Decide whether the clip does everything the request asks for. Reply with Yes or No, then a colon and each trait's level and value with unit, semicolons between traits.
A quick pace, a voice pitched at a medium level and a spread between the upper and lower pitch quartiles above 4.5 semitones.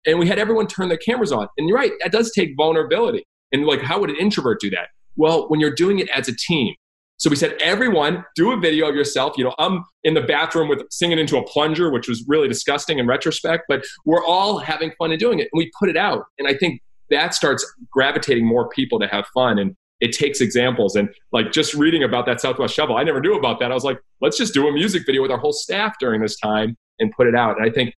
Yes: fast, 260 wpm; medium, 155 Hz; wide, 5.6 semitones